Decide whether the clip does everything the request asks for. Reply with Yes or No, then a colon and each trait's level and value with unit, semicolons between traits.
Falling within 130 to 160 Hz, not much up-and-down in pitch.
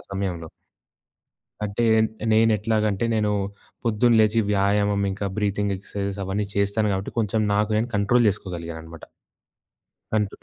No: low, 100 Hz; narrow, 1.6 semitones